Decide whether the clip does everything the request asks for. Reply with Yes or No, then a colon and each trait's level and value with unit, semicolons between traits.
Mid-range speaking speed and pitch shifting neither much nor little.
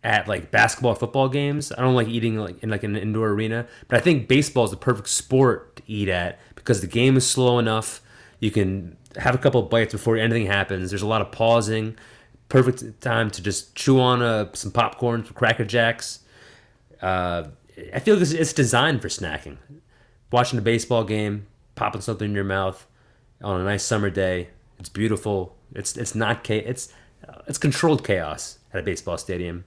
Yes: average, 190 wpm; average, 3.2 semitones